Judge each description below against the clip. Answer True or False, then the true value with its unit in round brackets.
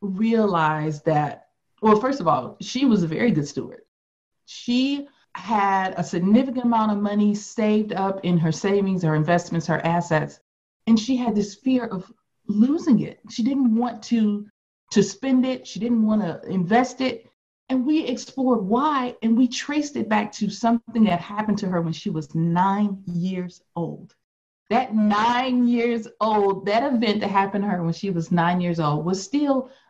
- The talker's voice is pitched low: False (210 Hz)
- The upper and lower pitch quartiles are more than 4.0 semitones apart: True (4.8 semitones)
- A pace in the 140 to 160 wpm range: False (175 wpm)